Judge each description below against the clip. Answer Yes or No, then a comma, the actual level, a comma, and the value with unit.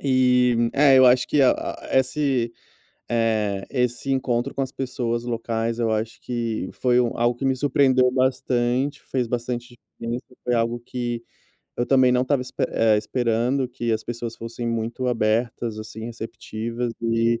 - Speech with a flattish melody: Yes, narrow, 1.8 semitones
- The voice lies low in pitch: Yes, low, 120 Hz